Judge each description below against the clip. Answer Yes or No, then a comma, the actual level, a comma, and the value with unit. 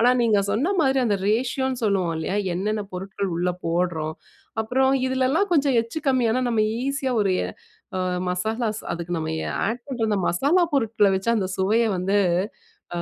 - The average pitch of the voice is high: Yes, high, 220 Hz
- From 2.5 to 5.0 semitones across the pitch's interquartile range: No, wide, 5.4 semitones